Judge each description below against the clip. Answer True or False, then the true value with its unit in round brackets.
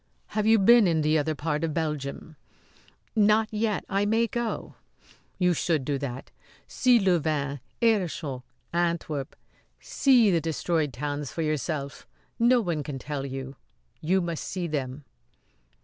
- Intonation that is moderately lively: False (5.7 semitones)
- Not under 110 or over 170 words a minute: True (140 wpm)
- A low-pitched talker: False (160 Hz)